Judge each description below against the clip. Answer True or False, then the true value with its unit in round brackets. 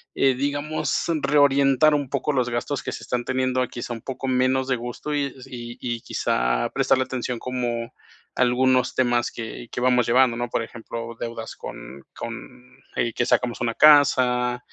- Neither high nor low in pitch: False (125 Hz)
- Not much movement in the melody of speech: True (1.8 semitones)